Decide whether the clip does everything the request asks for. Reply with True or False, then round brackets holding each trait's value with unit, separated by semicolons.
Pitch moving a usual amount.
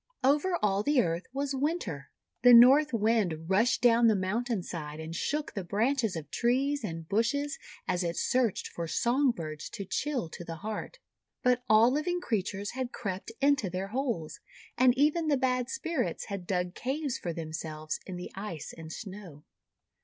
False (6.8 semitones)